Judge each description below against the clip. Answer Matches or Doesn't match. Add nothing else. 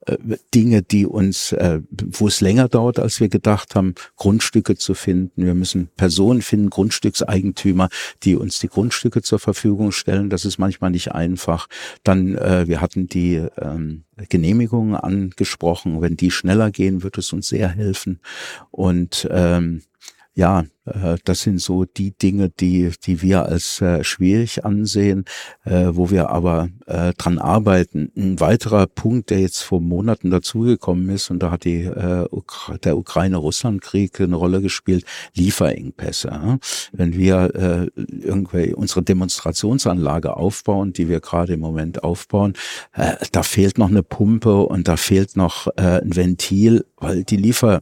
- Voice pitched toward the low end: Matches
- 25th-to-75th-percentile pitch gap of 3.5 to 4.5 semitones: Doesn't match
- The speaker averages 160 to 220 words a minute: Doesn't match